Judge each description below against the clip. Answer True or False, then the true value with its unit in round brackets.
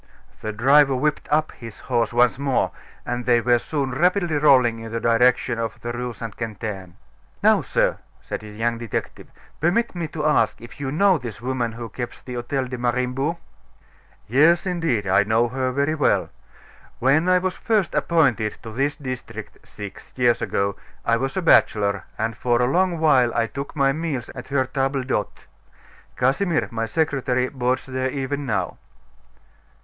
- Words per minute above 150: True (170 wpm)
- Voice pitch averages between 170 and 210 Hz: False (125 Hz)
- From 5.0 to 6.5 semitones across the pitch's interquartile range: False (3.9 semitones)